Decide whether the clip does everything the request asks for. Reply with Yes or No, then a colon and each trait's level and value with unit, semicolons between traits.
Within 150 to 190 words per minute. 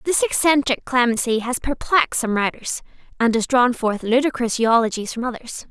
Yes: average, 160 wpm